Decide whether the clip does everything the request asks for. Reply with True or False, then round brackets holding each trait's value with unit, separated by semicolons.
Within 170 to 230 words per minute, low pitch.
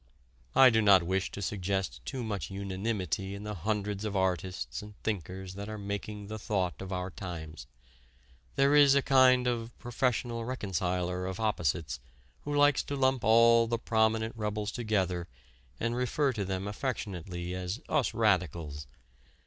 False (155 wpm; 105 Hz)